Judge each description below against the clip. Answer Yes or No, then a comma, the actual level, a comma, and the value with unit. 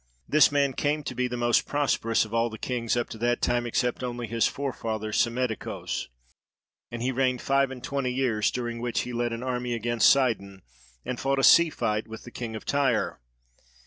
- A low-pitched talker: Yes, low, 120 Hz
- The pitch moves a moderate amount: No, narrow, 2.3 semitones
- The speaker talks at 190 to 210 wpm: Yes, average, 200 wpm